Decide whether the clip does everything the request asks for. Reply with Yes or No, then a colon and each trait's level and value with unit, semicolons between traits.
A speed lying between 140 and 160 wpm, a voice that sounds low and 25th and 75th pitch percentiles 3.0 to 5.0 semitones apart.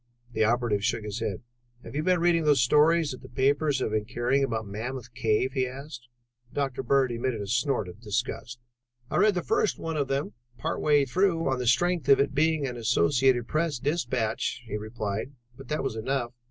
No: average, 200 wpm; low, 130 Hz; average, 3.8 semitones